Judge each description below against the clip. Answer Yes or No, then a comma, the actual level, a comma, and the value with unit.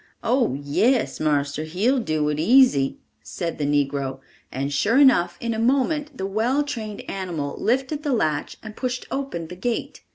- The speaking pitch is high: Yes, high, 205 Hz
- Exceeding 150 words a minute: Yes, average, 165 wpm